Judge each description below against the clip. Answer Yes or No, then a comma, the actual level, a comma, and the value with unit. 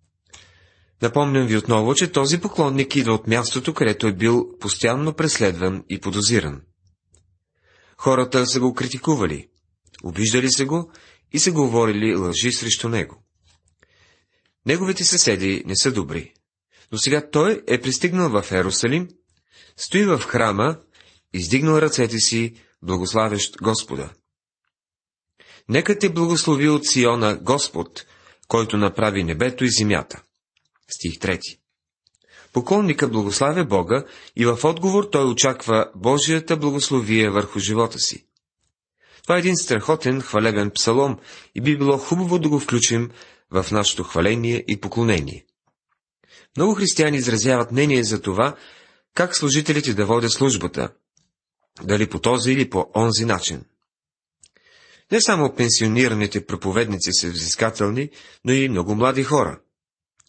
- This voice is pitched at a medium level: No, low, 115 Hz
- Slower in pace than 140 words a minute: Yes, average, 120 wpm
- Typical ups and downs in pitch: No, wide, 6.0 semitones